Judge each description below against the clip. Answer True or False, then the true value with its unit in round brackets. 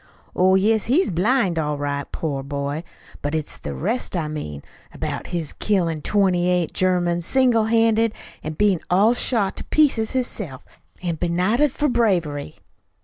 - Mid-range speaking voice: True (180 Hz)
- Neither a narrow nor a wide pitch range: False (6.2 semitones)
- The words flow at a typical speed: True (150 wpm)